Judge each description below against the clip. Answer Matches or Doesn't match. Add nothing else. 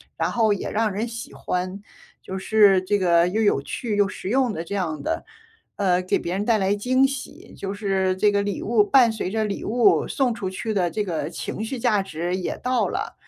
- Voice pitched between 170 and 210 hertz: Matches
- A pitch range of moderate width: Matches